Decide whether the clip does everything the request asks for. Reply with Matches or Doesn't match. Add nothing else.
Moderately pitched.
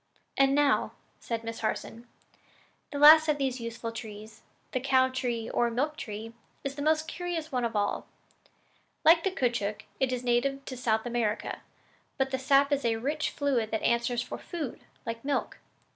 Doesn't match